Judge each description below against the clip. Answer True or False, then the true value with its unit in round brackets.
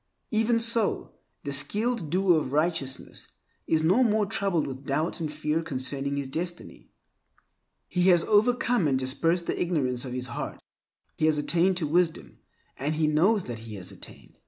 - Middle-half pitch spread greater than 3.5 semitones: True (5.2 semitones)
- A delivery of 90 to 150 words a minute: False (165 wpm)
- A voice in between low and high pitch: True (160 Hz)